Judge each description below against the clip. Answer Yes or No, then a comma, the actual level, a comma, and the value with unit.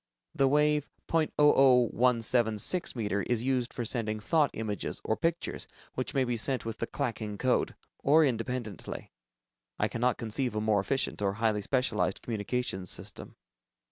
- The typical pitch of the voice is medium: No, low, 120 Hz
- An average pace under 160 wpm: Yes, average, 140 wpm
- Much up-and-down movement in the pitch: No, average, 3.8 semitones